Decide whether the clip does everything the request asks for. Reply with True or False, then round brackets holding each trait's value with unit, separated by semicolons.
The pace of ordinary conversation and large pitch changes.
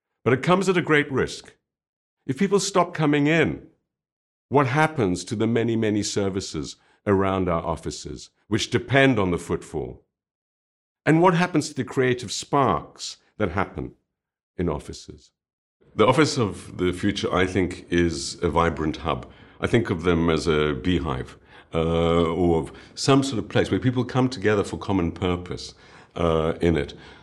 True (160 wpm; 7.4 semitones)